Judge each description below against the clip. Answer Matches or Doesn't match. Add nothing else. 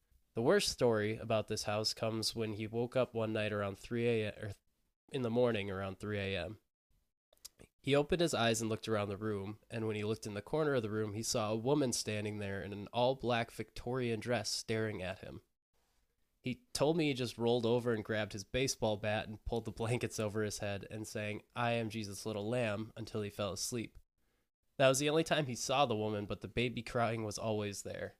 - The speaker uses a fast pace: Matches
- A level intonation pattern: Matches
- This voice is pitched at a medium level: Doesn't match